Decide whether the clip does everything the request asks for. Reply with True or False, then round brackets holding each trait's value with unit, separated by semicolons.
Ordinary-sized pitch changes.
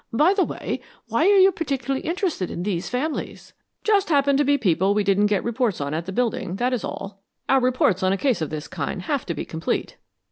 False (7.1 semitones)